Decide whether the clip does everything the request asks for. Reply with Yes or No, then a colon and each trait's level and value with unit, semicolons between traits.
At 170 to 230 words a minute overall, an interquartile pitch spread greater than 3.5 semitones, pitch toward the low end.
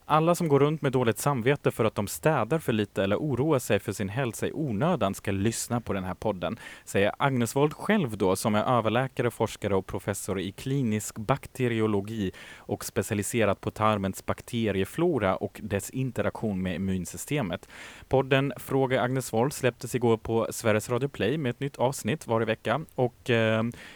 Yes: average, 175 wpm; average, 4.2 semitones; low, 115 Hz